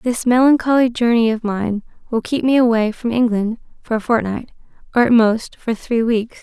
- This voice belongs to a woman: Yes, female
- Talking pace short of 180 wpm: No, average, 185 wpm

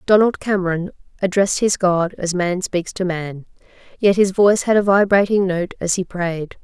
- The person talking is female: Yes, female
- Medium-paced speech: Yes, average, 180 wpm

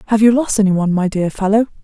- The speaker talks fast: Yes, fast, 230 wpm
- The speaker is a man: No, female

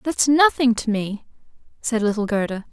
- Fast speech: No, average, 155 wpm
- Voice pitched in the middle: No, high, 235 Hz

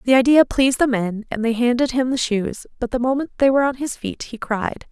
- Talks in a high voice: Yes, very high, 250 Hz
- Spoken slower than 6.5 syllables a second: Yes, 5.7 syllables/s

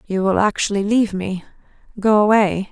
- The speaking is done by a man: No, female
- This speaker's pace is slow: Yes, slow, 130 wpm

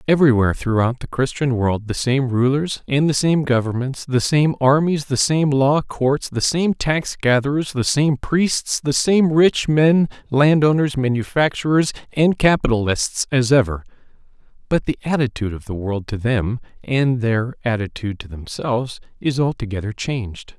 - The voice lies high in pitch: No, low, 130 Hz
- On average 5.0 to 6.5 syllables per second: No, 4.7 syllables/s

